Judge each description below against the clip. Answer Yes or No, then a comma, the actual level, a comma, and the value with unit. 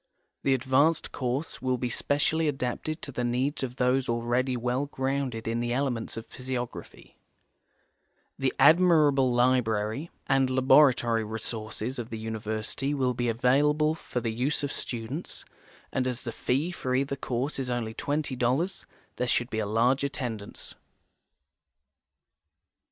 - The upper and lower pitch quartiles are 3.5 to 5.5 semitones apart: No, average, 2.7 semitones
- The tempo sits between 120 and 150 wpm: Yes, average, 140 wpm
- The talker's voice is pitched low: Yes, low, 125 Hz